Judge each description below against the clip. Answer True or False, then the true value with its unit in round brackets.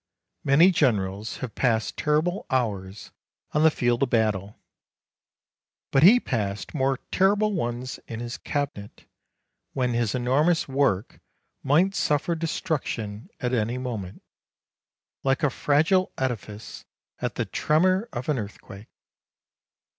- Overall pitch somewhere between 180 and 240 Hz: False (130 Hz)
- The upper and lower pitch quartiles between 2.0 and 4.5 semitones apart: False (5.5 semitones)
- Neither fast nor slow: False (125 wpm)